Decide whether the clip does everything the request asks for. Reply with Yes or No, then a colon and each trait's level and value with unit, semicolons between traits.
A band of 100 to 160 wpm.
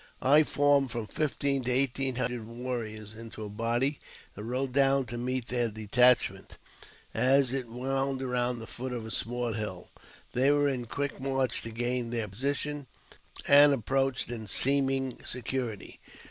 Yes: average, 155 wpm